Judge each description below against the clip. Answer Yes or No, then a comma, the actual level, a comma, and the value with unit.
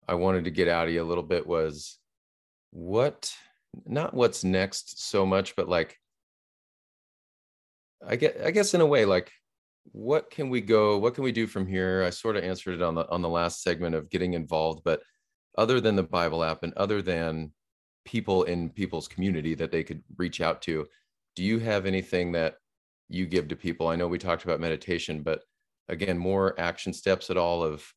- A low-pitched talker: Yes, very low, 90 Hz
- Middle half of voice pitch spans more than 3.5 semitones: No, average, 2.8 semitones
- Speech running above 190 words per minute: Yes, average, 200 wpm